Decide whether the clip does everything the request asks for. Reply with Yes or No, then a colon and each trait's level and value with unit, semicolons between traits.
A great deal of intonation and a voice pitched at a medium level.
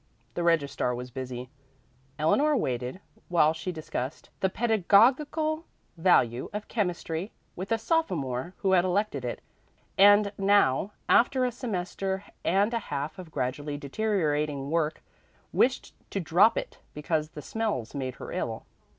Yes: wide, 6.4 semitones; medium, 175 Hz